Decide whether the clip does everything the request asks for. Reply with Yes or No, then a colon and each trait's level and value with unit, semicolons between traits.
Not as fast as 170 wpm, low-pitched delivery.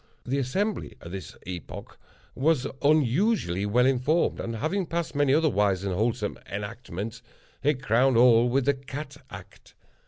Yes: average, 150 wpm; low, 125 Hz